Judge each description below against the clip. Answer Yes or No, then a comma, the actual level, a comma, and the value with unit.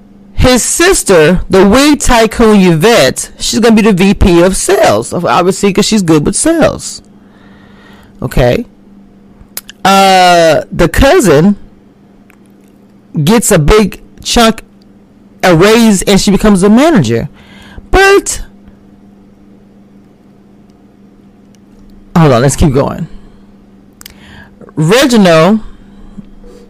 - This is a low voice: No, high, 190 Hz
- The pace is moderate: No, slow, 90 wpm